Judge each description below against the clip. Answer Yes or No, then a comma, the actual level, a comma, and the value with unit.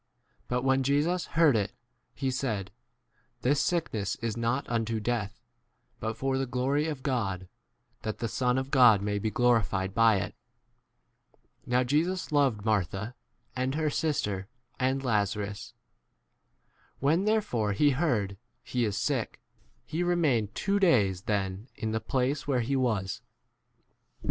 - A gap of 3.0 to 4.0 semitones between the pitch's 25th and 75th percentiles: No, average, 4.9 semitones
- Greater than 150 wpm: No, average, 145 wpm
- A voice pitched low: Yes, low, 125 Hz